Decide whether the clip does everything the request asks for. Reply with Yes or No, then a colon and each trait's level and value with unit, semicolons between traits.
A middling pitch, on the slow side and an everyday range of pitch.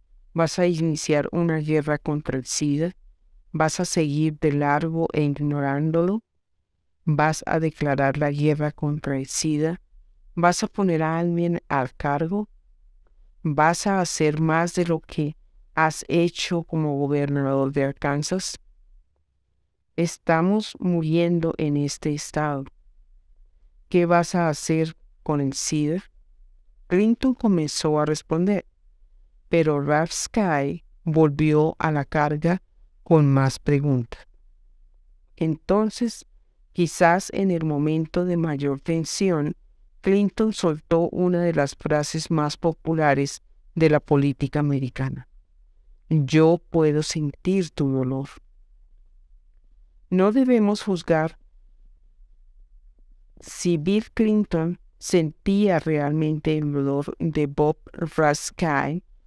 Yes: medium, 155 Hz; slow, 105 wpm; average, 3.6 semitones